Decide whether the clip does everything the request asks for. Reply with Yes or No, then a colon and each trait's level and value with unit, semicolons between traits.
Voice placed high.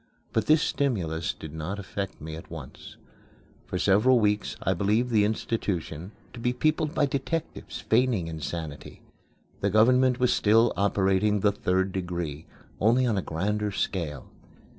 No: low, 100 Hz